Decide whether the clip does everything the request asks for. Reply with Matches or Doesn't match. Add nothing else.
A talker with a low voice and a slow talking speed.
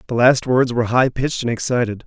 Doesn't match